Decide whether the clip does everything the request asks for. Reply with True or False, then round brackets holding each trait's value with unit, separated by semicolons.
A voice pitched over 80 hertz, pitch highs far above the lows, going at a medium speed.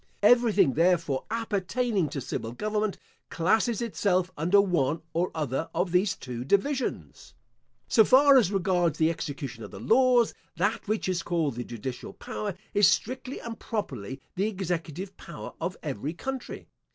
True (185 Hz; 5.8 semitones; 150 wpm)